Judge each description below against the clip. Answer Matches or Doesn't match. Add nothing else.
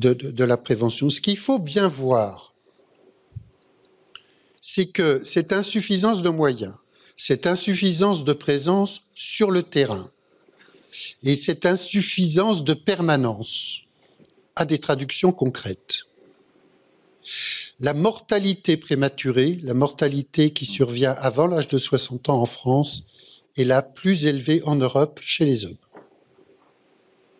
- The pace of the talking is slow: Matches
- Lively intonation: Matches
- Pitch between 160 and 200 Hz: Doesn't match